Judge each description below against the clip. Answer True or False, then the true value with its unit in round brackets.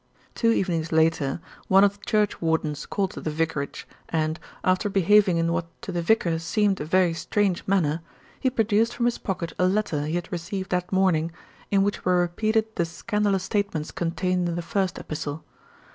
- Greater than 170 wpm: True (180 wpm)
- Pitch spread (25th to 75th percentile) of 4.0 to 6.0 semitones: False (3.6 semitones)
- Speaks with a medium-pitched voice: True (180 Hz)